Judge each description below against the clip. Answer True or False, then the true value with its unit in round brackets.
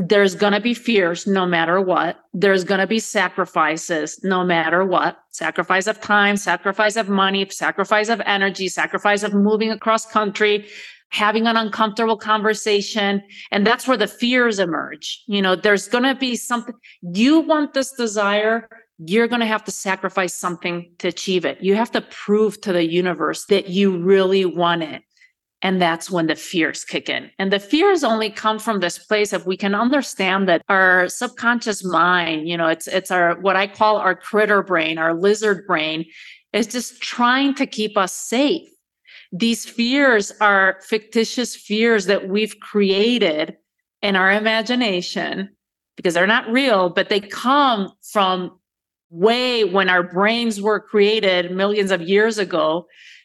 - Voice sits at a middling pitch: False (200 Hz)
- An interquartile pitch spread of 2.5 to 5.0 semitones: True (3.3 semitones)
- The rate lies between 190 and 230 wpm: False (165 wpm)